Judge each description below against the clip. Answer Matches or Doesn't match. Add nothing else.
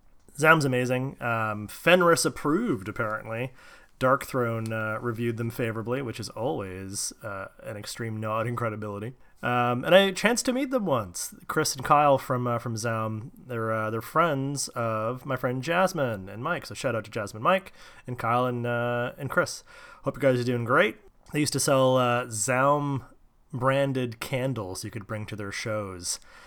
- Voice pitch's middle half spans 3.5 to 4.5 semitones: Matches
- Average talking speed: Matches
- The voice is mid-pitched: Doesn't match